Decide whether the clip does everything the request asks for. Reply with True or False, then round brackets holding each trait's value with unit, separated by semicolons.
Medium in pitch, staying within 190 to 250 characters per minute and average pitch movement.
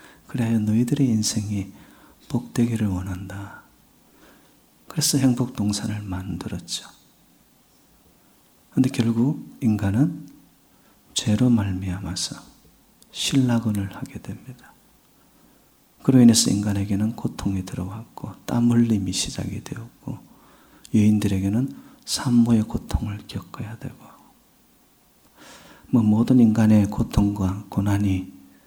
False (110 Hz; 230 characters per minute; 3.3 semitones)